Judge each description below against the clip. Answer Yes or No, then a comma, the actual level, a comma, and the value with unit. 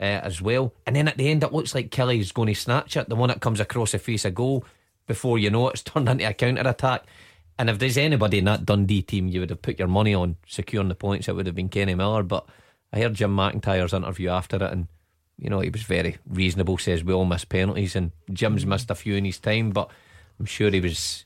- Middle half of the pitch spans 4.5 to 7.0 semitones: No, average, 3.9 semitones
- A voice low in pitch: Yes, low, 100 Hz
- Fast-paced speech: Yes, fast, 255 wpm